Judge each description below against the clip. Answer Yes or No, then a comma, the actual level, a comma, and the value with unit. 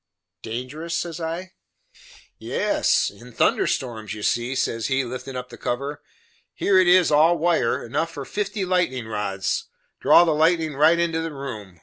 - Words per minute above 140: Yes, average, 160 wpm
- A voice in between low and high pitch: Yes, medium, 150 Hz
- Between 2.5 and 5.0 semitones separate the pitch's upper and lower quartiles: No, wide, 5.6 semitones